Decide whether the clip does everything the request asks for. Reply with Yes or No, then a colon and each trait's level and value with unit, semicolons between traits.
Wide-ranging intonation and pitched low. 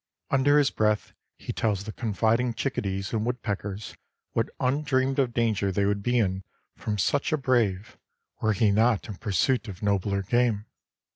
No: average, 3.6 semitones; low, 110 Hz